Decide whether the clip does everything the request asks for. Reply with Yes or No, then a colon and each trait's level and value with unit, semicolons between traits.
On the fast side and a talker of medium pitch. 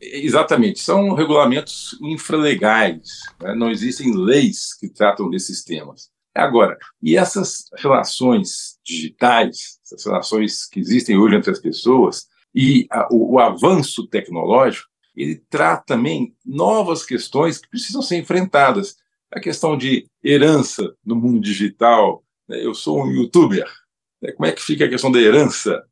No: average, 140 wpm; medium, 160 Hz